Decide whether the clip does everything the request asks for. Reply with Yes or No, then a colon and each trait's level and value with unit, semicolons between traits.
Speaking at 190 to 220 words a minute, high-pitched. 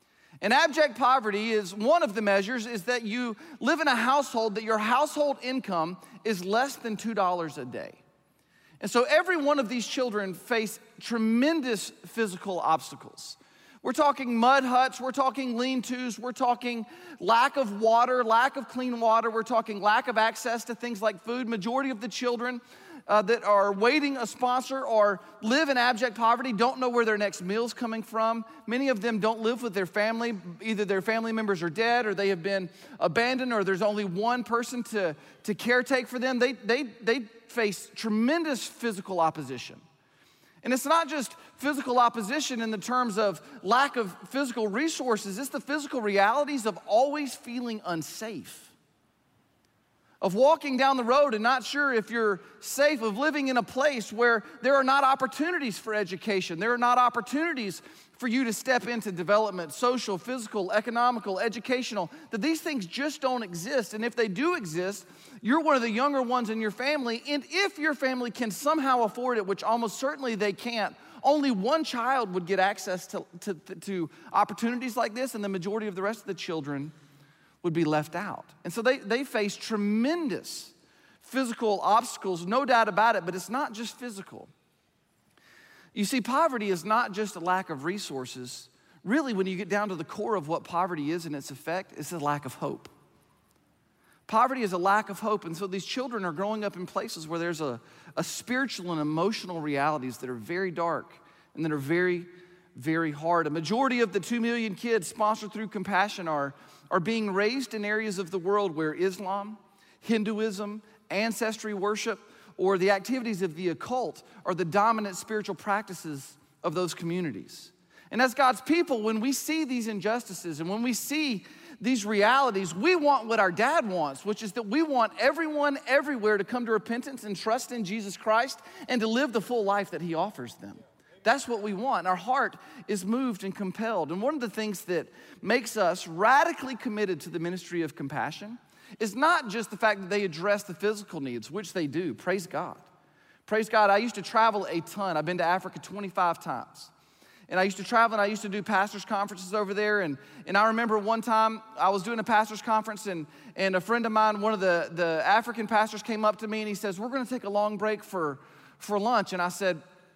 Yes: average, 195 wpm; high, 220 Hz